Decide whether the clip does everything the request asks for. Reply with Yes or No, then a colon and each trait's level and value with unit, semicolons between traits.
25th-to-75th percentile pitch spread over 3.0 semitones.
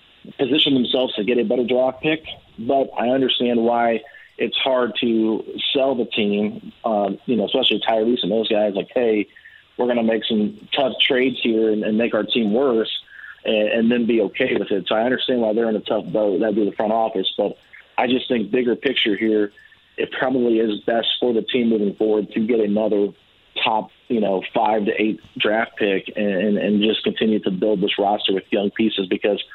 No: narrow, 2.6 semitones